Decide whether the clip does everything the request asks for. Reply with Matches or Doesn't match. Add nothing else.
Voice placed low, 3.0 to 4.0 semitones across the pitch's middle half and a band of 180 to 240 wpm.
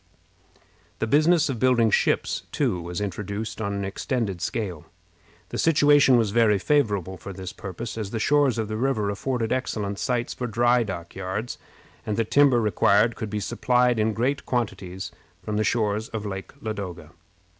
Doesn't match